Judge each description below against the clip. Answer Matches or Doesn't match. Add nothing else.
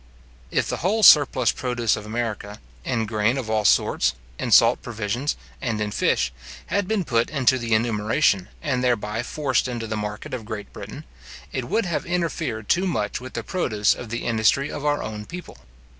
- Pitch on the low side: Matches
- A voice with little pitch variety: Doesn't match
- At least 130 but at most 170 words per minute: Doesn't match